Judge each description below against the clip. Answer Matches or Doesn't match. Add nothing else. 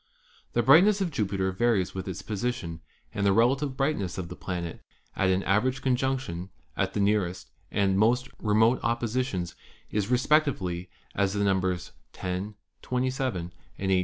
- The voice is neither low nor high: Doesn't match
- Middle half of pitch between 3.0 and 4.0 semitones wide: Doesn't match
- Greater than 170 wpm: Doesn't match